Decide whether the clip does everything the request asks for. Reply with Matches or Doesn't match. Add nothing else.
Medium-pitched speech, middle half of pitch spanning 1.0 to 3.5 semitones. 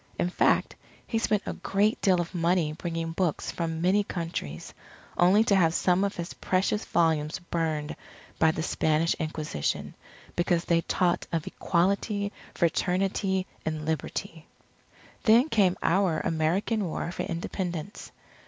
Matches